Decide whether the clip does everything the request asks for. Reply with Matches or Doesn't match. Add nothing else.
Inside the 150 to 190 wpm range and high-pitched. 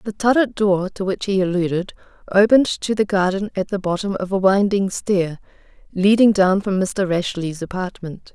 Matches